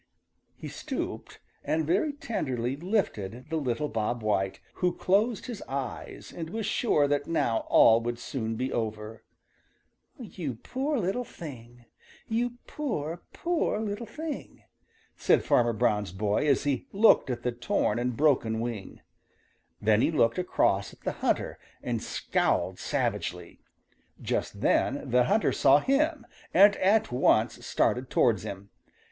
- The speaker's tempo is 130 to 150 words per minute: Yes, average, 140 wpm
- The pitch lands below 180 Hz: Yes, low, 135 Hz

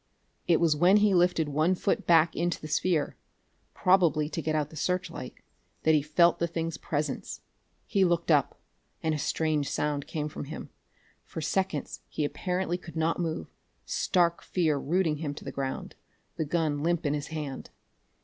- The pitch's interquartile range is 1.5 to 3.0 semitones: Yes, narrow, 2.6 semitones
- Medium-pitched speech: Yes, medium, 160 Hz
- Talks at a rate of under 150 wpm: No, average, 175 wpm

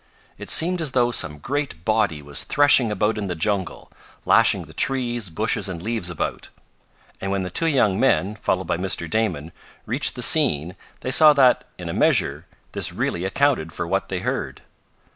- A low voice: Yes, low, 105 Hz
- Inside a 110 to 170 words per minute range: No, average, 180 wpm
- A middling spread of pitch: No, wide, 6.5 semitones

